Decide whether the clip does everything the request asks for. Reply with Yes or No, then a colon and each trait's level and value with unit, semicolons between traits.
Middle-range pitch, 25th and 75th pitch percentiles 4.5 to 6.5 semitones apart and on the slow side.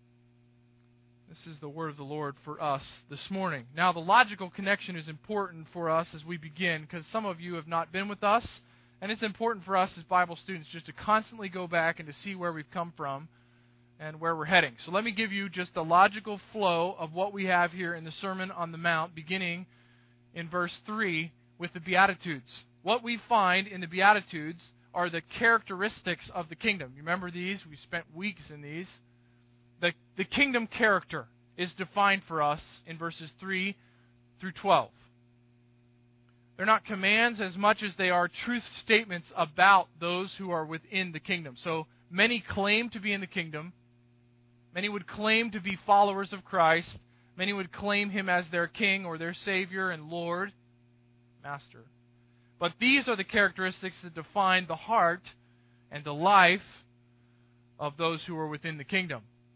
No: medium, 170 Hz; average, 5.3 semitones; average, 180 wpm